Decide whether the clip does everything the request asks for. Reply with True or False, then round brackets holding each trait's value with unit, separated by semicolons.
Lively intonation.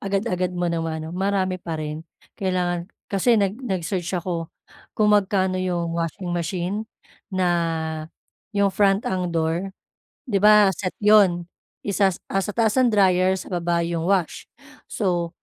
False (2.5 semitones)